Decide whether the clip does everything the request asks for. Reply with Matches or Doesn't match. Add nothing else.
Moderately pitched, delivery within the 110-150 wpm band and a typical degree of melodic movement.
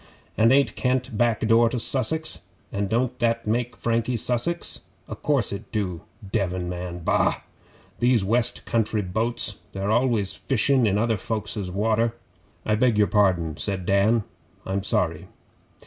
Doesn't match